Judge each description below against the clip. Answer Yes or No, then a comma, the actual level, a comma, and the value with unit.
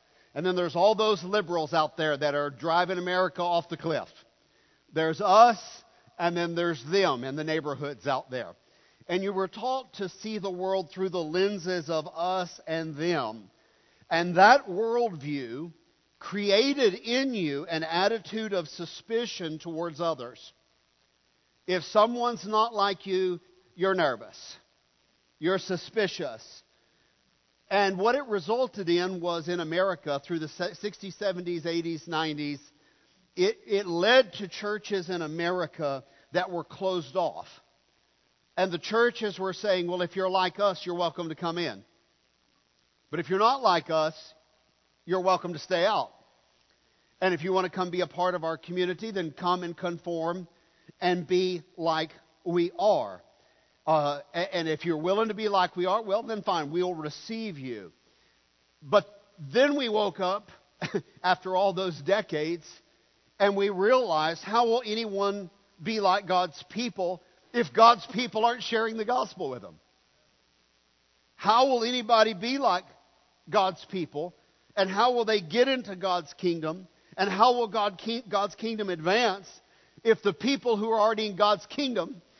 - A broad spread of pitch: No, average, 3.8 semitones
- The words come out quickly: No, average, 155 wpm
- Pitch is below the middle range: No, medium, 180 Hz